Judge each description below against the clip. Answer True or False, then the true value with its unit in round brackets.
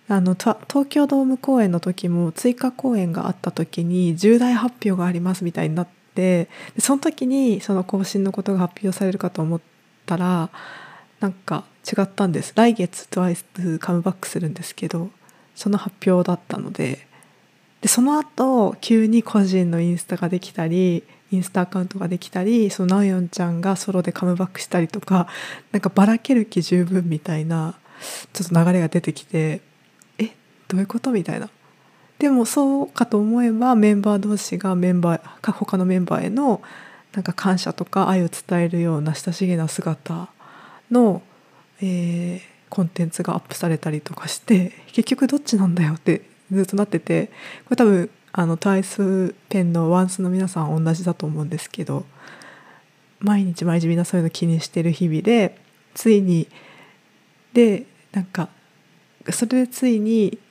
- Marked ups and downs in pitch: False (3.4 semitones)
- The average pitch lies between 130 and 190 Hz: True (185 Hz)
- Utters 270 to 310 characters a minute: False (335 characters per minute)